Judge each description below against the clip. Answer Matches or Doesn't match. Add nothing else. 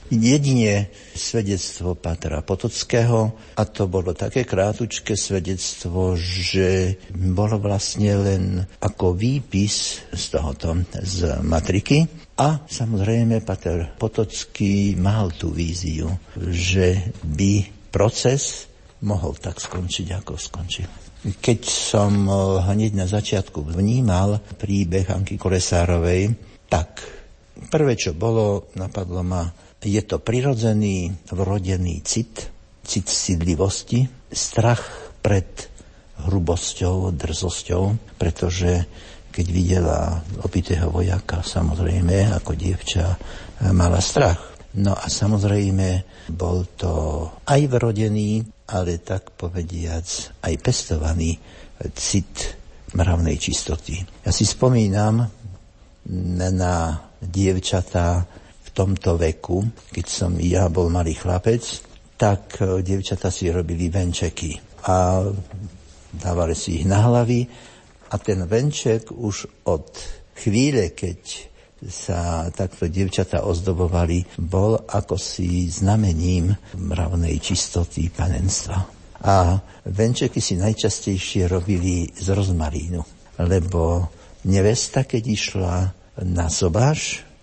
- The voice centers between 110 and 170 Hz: Doesn't match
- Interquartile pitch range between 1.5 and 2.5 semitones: Doesn't match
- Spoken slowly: Matches